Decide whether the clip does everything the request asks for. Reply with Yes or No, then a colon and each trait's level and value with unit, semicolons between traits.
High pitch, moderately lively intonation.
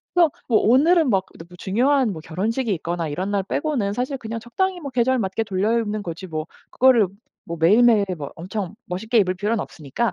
Yes: high, 215 Hz; average, 5.0 semitones